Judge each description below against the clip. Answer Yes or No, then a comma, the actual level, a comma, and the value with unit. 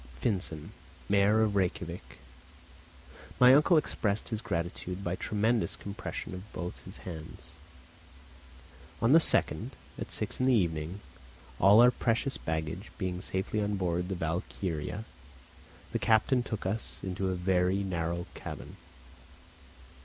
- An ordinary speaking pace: No, slow, 130 wpm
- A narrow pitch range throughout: No, average, 3.8 semitones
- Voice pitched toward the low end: Yes, very low, 95 Hz